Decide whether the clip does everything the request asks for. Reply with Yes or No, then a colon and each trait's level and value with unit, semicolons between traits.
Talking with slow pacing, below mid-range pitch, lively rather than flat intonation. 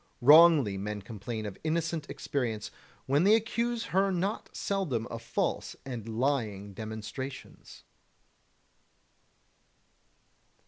Yes: slow, 95 wpm; low, 130 Hz; wide, 7.7 semitones